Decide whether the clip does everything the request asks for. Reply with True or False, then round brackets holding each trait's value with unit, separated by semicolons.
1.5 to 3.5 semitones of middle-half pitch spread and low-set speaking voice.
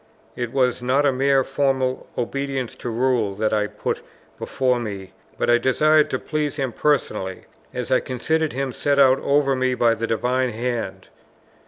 True (2.4 semitones; 130 Hz)